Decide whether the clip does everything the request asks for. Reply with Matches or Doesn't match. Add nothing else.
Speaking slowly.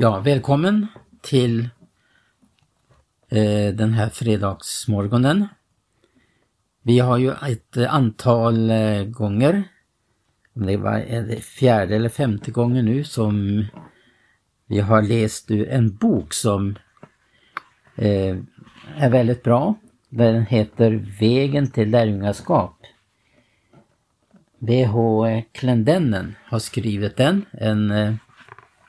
Matches